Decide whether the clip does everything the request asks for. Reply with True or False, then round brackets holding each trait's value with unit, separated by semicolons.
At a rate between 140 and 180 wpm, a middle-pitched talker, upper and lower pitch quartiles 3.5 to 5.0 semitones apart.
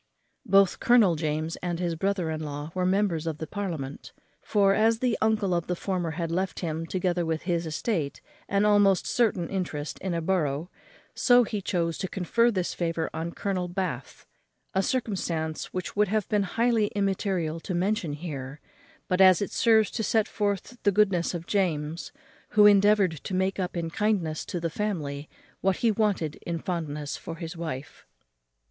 True (175 wpm; 180 Hz; 3.8 semitones)